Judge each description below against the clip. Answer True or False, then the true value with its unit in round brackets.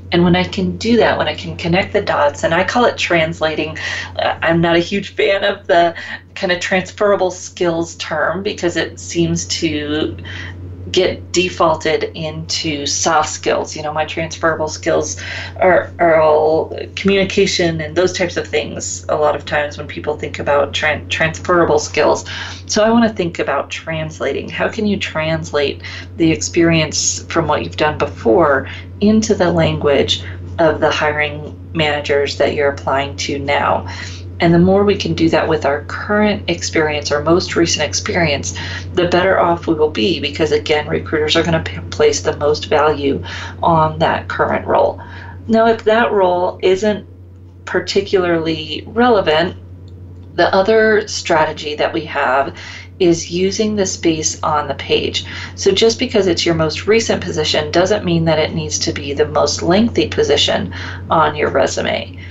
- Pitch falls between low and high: True (155 Hz)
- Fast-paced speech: False (165 wpm)